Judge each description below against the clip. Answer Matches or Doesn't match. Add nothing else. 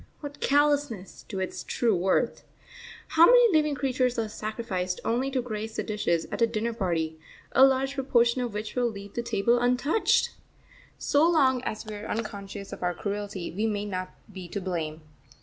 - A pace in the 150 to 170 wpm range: Doesn't match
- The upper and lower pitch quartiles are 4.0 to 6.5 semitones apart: Matches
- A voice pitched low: Doesn't match